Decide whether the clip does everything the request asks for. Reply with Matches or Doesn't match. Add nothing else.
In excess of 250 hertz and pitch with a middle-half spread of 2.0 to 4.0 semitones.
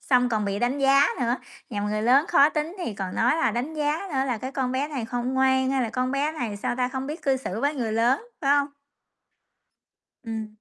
Matches